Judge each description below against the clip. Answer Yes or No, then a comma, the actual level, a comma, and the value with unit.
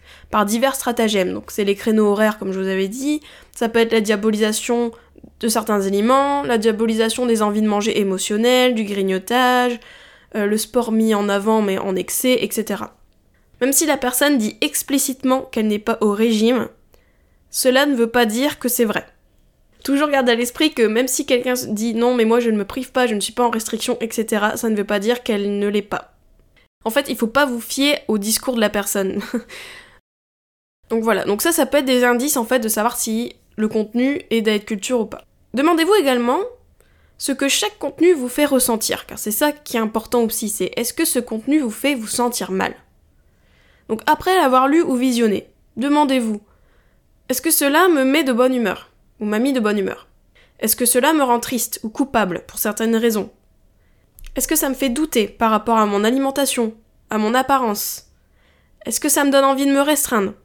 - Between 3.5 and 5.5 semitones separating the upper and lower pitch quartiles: Yes, average, 3.8 semitones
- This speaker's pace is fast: No, average, 205 wpm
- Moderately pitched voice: No, high, 235 Hz